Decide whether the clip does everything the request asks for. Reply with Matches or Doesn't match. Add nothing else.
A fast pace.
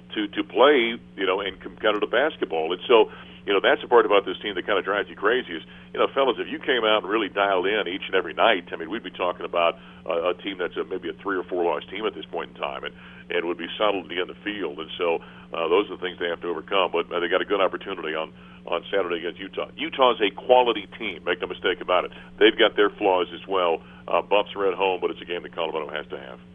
Matches